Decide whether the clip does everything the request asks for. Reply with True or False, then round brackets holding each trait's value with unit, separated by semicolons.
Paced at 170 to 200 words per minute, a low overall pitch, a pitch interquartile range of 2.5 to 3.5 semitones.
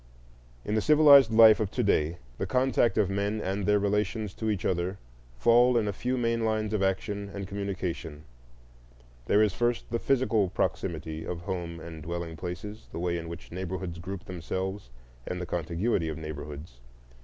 False (175 wpm; 95 Hz; 4.1 semitones)